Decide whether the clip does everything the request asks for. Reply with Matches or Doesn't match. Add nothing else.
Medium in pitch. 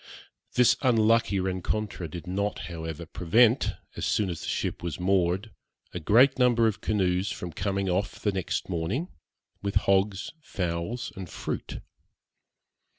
Doesn't match